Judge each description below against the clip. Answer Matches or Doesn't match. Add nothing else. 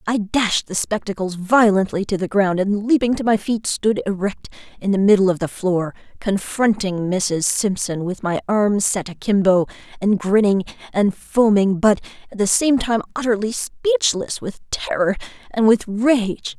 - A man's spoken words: Doesn't match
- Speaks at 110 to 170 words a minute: Matches